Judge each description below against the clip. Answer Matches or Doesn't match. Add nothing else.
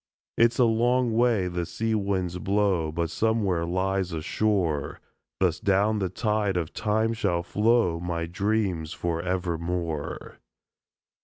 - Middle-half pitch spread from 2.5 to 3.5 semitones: Doesn't match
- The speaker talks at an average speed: Doesn't match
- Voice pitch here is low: Matches